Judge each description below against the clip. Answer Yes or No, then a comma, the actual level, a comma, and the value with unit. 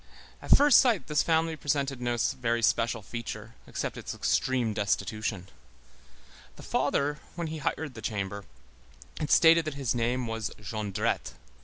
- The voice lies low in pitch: Yes, low, 120 Hz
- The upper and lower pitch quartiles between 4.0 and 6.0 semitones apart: Yes, wide, 5.4 semitones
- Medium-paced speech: Yes, average, 145 wpm